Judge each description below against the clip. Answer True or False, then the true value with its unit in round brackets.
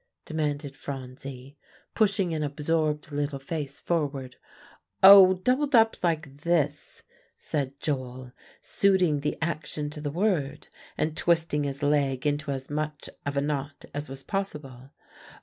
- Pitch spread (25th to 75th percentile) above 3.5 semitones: False (2.9 semitones)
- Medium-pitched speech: True (150 Hz)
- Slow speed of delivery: True (130 wpm)